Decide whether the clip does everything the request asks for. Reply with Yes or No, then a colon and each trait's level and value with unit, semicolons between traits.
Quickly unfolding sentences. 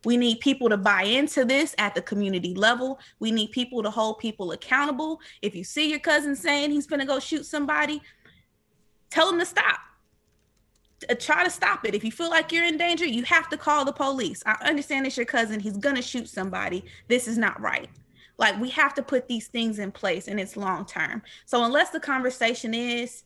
Yes: fast, 215 wpm